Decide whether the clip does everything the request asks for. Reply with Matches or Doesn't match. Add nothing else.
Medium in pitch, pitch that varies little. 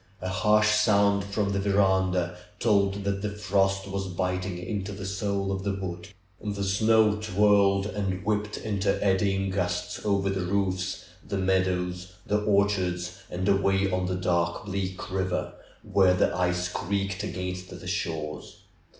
Doesn't match